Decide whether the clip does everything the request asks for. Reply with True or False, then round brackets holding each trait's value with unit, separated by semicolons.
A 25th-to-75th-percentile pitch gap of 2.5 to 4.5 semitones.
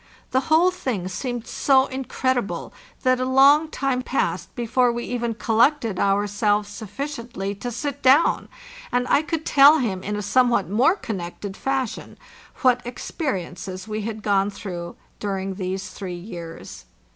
False (5.0 semitones)